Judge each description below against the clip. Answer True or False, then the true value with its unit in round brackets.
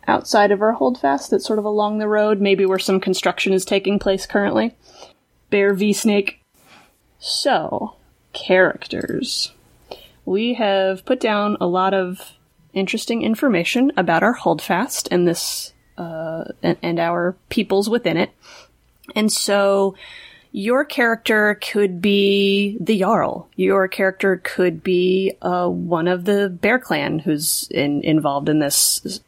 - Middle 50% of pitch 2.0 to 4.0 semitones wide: True (2.9 semitones)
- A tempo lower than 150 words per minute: True (135 wpm)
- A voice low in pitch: False (195 Hz)